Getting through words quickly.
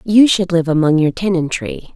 No: average, 185 wpm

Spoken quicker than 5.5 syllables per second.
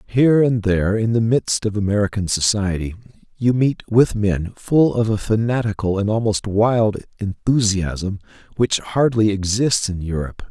No: 4.6 syllables/s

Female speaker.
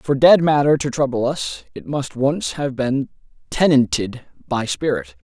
No: male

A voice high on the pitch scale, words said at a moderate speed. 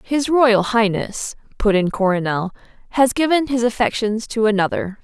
Yes: high, 225 Hz; average, 145 wpm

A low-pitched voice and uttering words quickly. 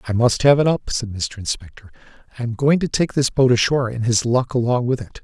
Yes: low, 120 Hz; fast, 250 wpm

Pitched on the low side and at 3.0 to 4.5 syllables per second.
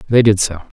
No: low, 105 Hz; 5.8 syllables/s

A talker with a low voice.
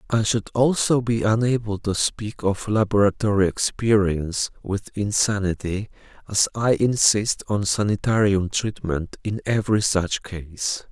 Yes: low, 105 Hz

